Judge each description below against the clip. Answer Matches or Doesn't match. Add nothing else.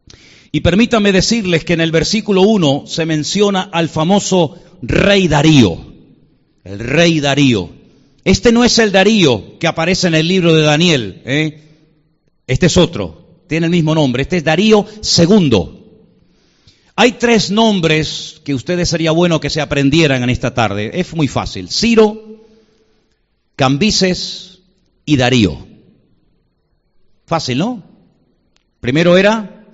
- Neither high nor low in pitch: Matches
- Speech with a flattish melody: Doesn't match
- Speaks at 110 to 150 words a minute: Matches